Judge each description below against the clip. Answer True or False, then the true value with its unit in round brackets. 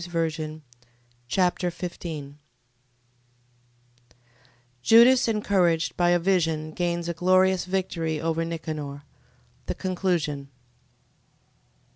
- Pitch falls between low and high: True (170 Hz)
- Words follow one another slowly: True (85 wpm)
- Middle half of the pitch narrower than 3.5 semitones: True (2.7 semitones)